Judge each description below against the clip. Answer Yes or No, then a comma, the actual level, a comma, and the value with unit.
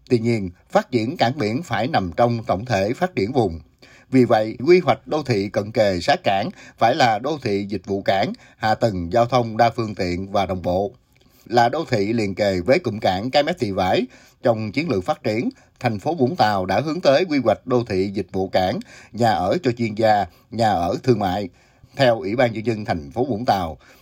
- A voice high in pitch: No, low, 115 Hz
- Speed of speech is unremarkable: Yes, average, 225 wpm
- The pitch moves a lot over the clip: No, average, 4.0 semitones